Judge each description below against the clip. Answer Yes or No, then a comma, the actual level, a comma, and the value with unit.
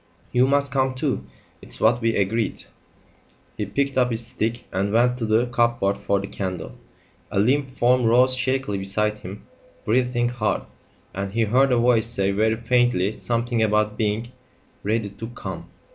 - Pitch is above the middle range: No, low, 115 Hz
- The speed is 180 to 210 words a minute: No, average, 165 wpm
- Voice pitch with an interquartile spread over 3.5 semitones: No, average, 2.9 semitones